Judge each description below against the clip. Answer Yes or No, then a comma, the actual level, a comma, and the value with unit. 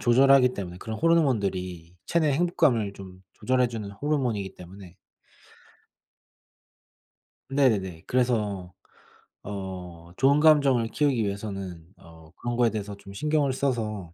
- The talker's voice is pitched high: No, low, 110 Hz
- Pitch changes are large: Yes, wide, 5.9 semitones